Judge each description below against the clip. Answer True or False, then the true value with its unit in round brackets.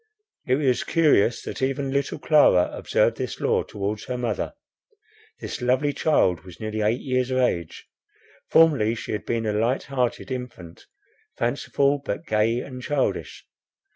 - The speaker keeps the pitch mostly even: False (4.2 semitones)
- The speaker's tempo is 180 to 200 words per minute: False (150 wpm)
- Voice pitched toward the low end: True (125 Hz)